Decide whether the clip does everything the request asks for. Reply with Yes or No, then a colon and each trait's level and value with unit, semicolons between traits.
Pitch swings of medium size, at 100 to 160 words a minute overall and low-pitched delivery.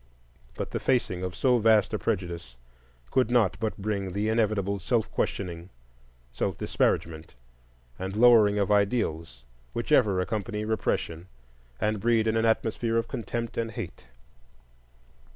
Yes: average, 3.6 semitones; slow, 135 wpm; low, 105 Hz